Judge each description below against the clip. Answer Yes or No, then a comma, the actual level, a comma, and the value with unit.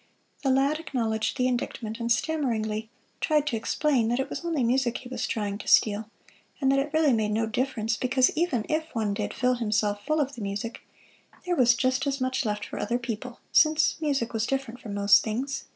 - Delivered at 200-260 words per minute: Yes, fast, 205 wpm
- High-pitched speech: Yes, high, 245 Hz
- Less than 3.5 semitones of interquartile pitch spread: No, average, 3.8 semitones